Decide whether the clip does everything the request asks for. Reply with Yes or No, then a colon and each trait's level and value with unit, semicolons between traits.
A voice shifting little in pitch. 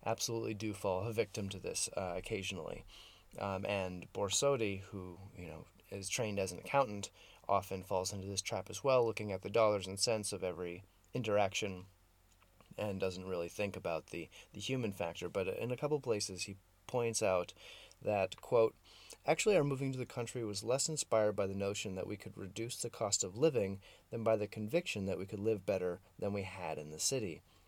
No: average, 3.3 semitones